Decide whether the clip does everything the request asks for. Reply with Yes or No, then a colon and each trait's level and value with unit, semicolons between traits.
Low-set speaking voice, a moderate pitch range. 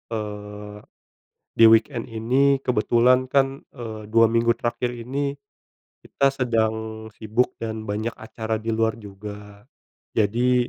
No: low, 115 Hz; narrow, 2.3 semitones